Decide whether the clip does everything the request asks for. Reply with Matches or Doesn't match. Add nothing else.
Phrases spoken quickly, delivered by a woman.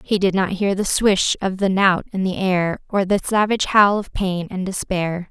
Matches